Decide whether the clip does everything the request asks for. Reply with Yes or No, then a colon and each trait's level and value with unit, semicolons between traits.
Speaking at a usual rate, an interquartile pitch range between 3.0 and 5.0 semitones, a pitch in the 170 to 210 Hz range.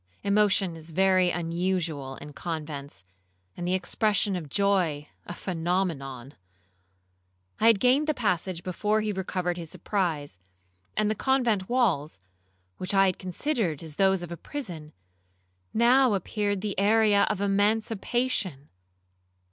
No: slow, 130 wpm; average, 4.2 semitones; high, 190 Hz